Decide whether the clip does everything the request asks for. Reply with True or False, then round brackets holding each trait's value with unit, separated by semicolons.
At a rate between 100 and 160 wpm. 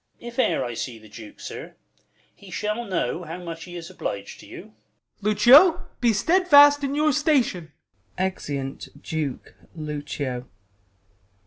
True (140 wpm)